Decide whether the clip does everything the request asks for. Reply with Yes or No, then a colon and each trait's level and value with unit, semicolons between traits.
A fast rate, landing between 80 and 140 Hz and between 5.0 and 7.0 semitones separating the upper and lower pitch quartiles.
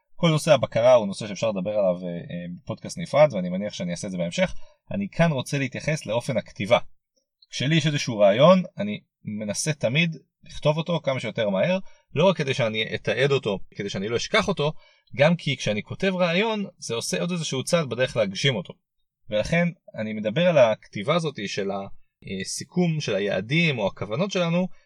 No: fast, 175 wpm; medium, 170 Hz; wide, 5.4 semitones